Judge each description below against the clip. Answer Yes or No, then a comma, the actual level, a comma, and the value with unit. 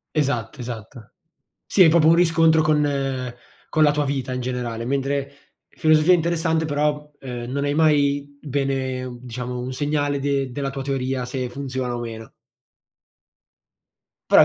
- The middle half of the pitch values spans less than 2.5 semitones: No, average, 2.8 semitones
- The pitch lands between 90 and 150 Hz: Yes, medium, 140 Hz